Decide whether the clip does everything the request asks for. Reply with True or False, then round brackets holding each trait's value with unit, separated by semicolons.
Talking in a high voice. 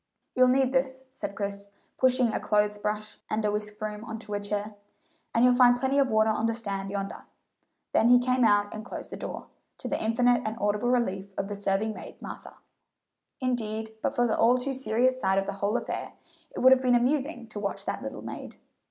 True (220 Hz)